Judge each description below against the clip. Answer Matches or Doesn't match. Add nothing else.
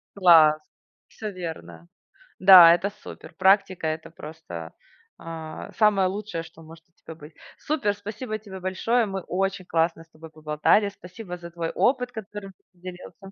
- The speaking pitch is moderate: Matches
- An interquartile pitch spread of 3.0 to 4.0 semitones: Matches